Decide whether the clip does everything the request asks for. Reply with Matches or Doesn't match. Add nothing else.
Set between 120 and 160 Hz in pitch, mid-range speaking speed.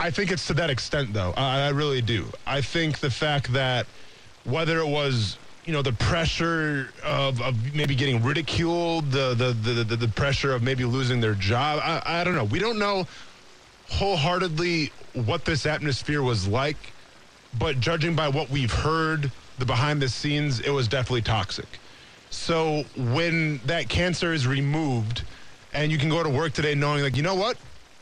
Matches